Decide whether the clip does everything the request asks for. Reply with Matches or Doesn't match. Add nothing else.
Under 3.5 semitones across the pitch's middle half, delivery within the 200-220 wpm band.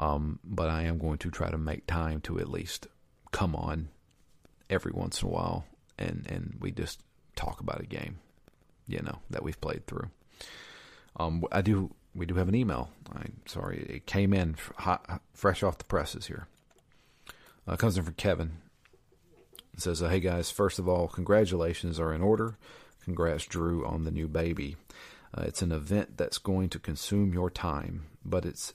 Doesn't match